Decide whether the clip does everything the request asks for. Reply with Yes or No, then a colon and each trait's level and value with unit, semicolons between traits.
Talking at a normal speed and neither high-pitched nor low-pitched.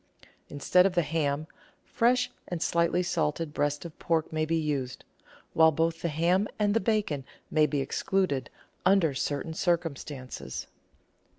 Yes: average, 150 wpm; medium, 160 Hz